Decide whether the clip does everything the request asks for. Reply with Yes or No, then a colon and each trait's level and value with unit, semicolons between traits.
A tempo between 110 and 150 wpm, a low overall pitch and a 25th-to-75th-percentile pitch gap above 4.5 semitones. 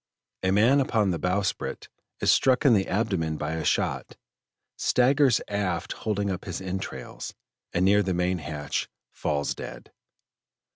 No: average, 145 wpm; very low, 95 Hz; average, 3.5 semitones